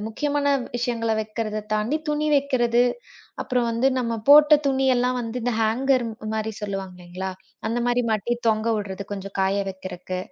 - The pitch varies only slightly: No, average, 3.3 semitones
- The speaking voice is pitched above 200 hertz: Yes, high, 230 Hz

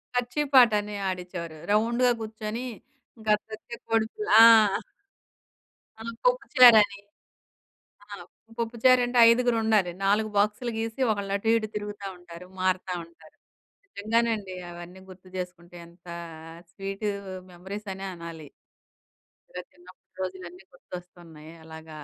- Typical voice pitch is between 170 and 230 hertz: Yes, high, 205 Hz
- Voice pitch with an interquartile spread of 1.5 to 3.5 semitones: No, average, 4.0 semitones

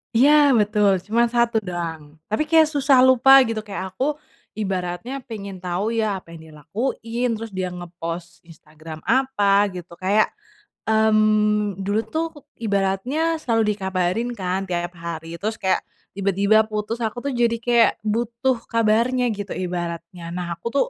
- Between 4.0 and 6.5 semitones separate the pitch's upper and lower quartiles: Yes, average, 4.4 semitones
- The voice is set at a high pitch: Yes, high, 210 Hz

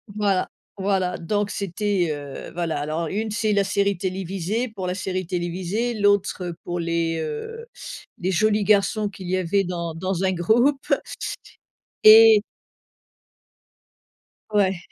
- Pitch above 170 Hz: Yes, high, 190 Hz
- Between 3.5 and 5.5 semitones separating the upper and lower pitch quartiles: No, average, 3.1 semitones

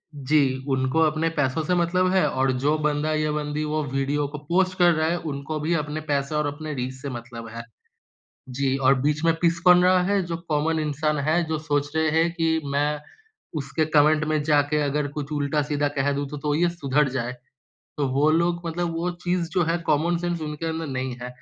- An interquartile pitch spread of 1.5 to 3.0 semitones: Yes, narrow, 2.5 semitones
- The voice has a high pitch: No, medium, 150 Hz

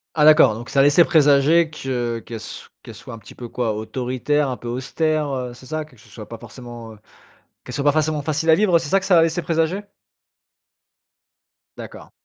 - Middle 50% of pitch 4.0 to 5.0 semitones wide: Yes, average, 4.7 semitones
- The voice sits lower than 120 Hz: No, medium, 140 Hz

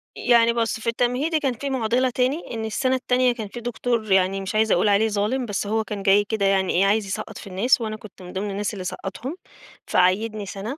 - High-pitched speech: Yes, high, 220 Hz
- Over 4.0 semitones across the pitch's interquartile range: No, average, 3.5 semitones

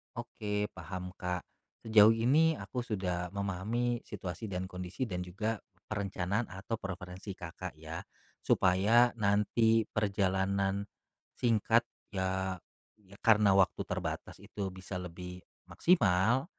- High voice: No, low, 100 Hz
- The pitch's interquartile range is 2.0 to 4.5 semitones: Yes, average, 3.2 semitones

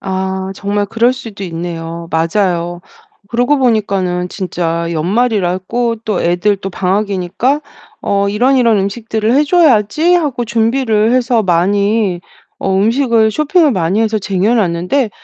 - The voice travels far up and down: No, average, 4.5 semitones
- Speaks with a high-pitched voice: Yes, high, 205 Hz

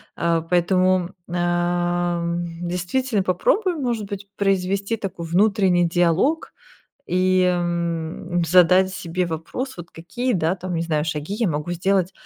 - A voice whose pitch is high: No, medium, 180 Hz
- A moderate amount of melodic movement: No, narrow, 2.3 semitones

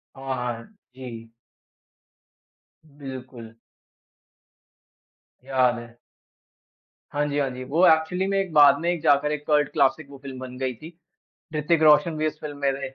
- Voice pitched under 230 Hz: Yes, medium, 140 Hz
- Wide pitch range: No, average, 2.9 semitones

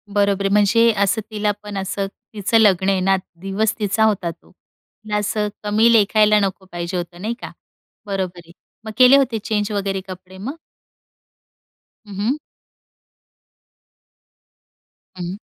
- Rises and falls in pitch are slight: Yes, narrow, 2.2 semitones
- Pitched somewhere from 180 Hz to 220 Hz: Yes, high, 205 Hz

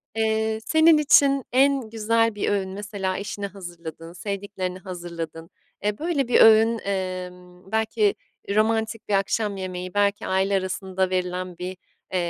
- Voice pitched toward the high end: Yes, high, 200 Hz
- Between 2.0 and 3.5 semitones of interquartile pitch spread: Yes, average, 3.2 semitones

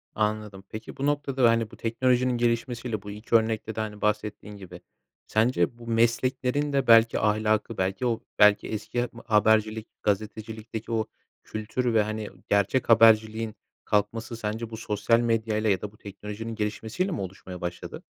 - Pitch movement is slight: Yes, narrow, 1.7 semitones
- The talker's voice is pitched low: Yes, low, 110 Hz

